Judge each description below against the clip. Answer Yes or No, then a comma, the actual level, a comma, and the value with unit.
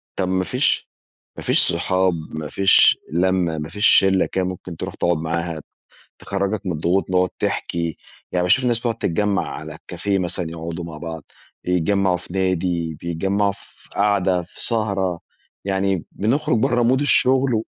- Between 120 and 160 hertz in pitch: No, very low, 95 Hz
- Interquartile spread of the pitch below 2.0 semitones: No, average, 2.9 semitones